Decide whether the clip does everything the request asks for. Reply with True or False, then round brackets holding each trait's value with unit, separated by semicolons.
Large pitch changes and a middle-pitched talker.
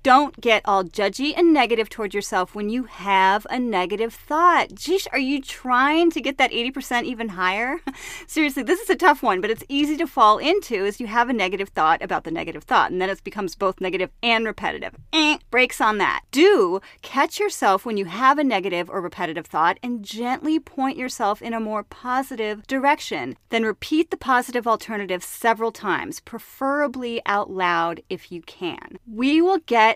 False (5.8 semitones; 240 Hz)